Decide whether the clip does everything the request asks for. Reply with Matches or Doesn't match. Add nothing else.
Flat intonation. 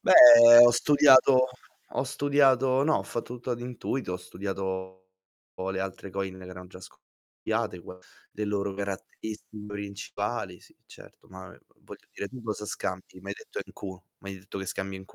Doesn't match